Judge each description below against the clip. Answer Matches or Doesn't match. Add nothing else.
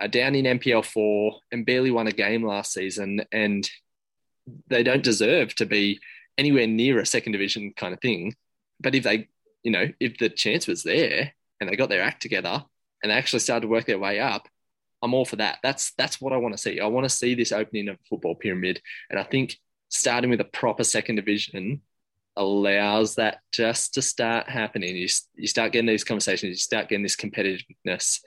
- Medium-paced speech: Doesn't match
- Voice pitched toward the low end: Matches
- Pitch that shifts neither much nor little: Matches